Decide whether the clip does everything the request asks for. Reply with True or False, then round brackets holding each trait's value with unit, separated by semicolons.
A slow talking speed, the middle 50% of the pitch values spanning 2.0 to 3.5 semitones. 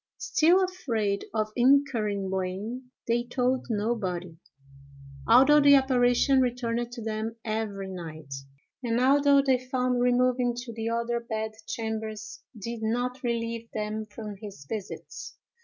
True (125 wpm; 2.7 semitones)